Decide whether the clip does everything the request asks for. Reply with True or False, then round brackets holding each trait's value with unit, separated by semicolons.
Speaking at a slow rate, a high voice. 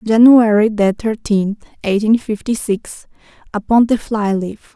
True (115 wpm; 215 Hz)